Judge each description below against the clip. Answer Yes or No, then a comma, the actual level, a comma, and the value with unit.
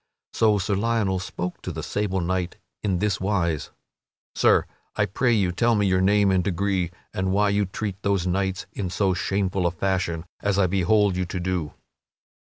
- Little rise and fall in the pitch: Yes, narrow, 2.0 semitones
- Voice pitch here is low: Yes, very low, 95 Hz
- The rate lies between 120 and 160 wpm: No, average, 180 wpm